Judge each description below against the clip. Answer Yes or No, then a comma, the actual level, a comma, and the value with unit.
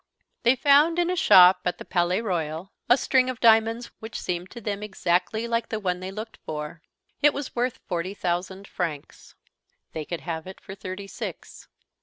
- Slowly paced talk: No, average, 185 wpm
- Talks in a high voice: Yes, high, 195 Hz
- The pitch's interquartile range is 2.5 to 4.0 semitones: No, average, 4.8 semitones